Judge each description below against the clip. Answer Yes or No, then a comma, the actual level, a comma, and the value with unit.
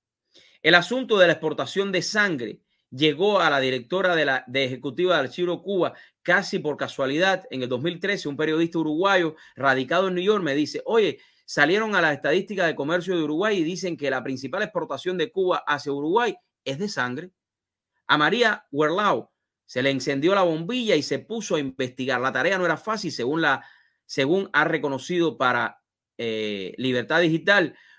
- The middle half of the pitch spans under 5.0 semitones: No, wide, 5.6 semitones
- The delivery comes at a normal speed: Yes, average, 175 wpm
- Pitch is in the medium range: Yes, medium, 160 Hz